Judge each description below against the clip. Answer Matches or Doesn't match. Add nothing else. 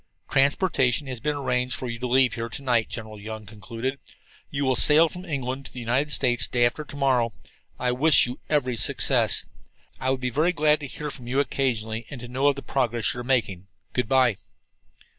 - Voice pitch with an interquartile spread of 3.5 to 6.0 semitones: Doesn't match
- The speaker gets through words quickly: Matches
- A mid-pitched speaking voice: Doesn't match